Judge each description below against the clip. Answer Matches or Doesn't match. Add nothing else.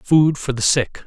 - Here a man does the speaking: Matches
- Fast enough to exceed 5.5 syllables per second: Doesn't match